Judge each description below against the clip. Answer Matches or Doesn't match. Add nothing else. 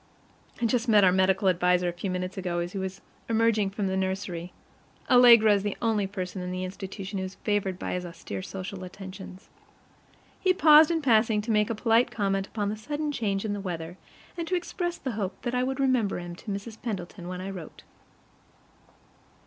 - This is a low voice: Doesn't match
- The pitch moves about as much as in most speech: Matches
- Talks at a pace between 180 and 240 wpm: Matches